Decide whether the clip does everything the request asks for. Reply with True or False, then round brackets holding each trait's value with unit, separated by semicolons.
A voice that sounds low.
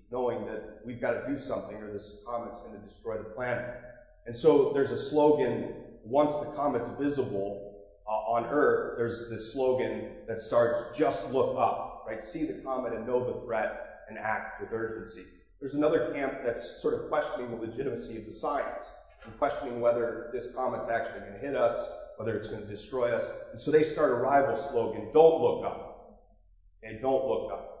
True (120 Hz)